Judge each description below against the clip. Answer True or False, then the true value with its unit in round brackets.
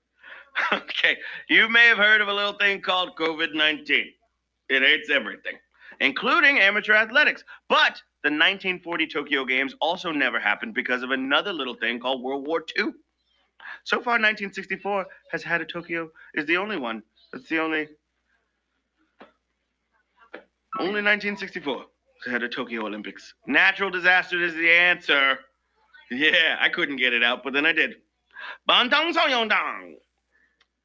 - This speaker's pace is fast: False (140 wpm)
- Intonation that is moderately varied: False (6.0 semitones)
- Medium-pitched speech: True (175 Hz)